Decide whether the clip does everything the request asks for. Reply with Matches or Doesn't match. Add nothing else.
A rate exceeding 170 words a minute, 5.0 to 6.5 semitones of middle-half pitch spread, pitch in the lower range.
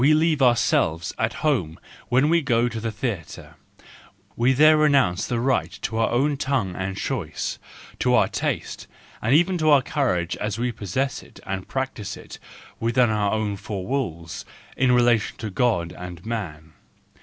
Doesn't match